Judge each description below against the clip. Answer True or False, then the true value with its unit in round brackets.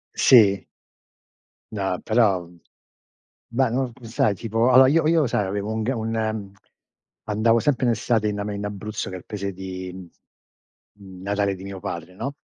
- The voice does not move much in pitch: False (3.1 semitones)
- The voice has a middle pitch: False (105 Hz)